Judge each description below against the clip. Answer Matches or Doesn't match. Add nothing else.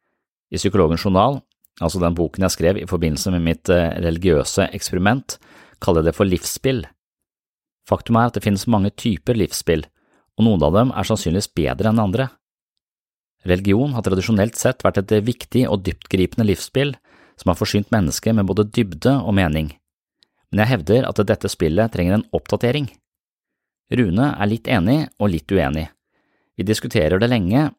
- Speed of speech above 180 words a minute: Doesn't match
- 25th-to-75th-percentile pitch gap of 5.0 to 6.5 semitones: Doesn't match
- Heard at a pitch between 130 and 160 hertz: Doesn't match